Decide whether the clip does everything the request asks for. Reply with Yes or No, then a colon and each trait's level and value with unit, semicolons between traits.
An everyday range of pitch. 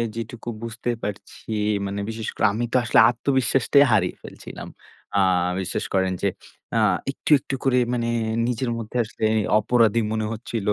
No: narrow, 2.3 semitones